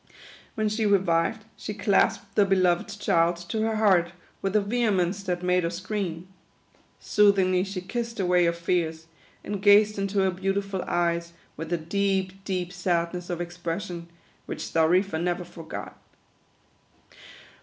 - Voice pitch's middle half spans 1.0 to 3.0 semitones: Yes, narrow, 2.6 semitones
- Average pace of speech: Yes, average, 145 wpm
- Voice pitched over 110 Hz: Yes, medium, 185 Hz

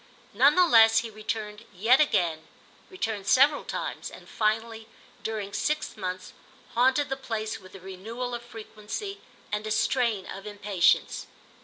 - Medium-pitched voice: No, high, 220 Hz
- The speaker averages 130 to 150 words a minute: Yes, average, 145 wpm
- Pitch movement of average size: Yes, average, 3.1 semitones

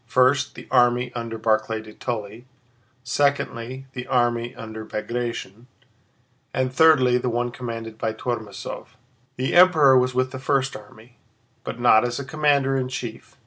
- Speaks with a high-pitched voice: No, low, 120 Hz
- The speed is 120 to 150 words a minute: Yes, average, 145 wpm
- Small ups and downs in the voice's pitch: Yes, narrow, 2.1 semitones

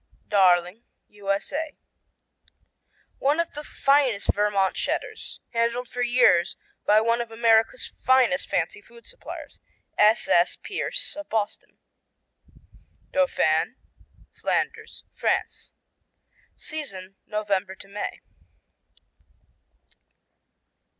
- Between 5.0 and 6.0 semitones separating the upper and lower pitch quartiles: Yes, wide, 5.5 semitones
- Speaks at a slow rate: Yes, slow, 85 wpm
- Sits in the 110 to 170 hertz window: No, high, 225 Hz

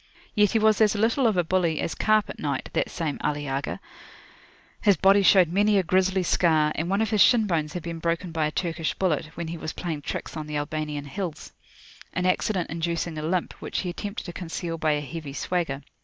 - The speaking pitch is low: No, medium, 170 Hz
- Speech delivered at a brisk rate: Yes, fast, 215 wpm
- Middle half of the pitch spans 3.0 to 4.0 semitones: Yes, average, 3.7 semitones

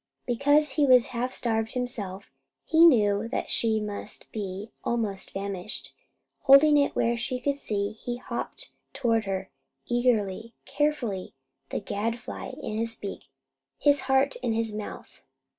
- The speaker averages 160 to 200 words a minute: No, average, 140 wpm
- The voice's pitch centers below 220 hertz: No, high, 230 Hz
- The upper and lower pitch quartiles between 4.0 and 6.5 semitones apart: No, average, 3.6 semitones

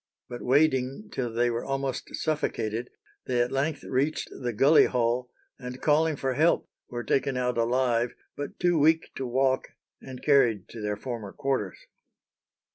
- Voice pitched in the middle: No, low, 130 Hz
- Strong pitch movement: No, narrow, 2.5 semitones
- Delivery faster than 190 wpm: No, average, 155 wpm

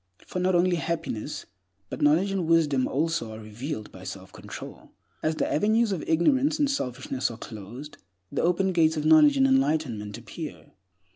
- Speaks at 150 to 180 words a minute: Yes, average, 165 wpm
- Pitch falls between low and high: Yes, medium, 160 Hz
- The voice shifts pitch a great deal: Yes, wide, 6.6 semitones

